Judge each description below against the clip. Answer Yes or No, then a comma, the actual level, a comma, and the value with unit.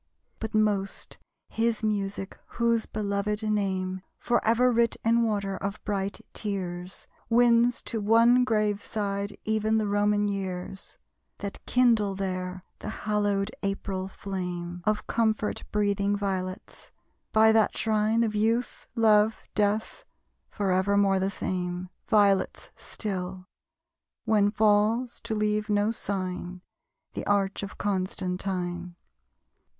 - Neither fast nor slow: No, slow, 115 wpm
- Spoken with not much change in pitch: Yes, narrow, 2.1 semitones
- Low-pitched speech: No, high, 205 Hz